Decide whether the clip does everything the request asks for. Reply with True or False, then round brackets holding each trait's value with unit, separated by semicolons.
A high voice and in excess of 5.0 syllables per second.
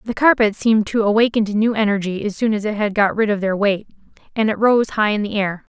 True (210 Hz; 6.2 syllables/s)